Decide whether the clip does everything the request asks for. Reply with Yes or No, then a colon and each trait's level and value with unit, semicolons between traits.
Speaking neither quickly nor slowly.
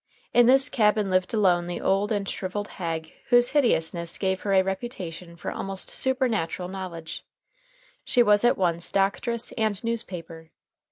Yes: average, 150 wpm